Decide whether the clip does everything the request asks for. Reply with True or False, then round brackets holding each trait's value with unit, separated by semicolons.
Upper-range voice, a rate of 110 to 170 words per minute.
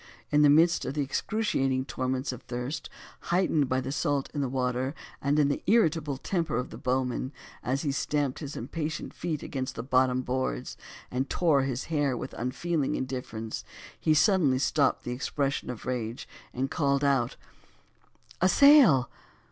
False (135 Hz; 155 wpm)